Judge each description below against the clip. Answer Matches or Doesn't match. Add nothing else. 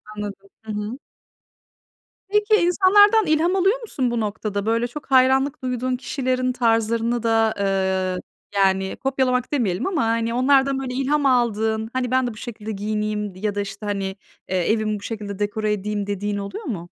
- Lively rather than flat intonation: Doesn't match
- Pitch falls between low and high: Doesn't match